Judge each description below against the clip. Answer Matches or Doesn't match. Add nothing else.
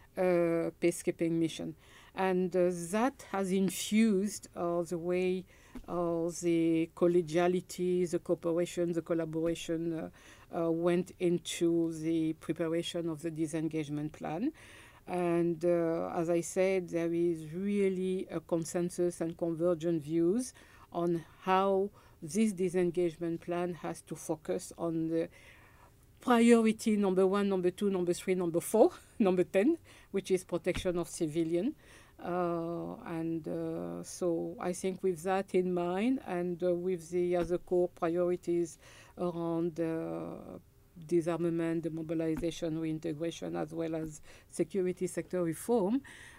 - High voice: Doesn't match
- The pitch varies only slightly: Matches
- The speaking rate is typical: Doesn't match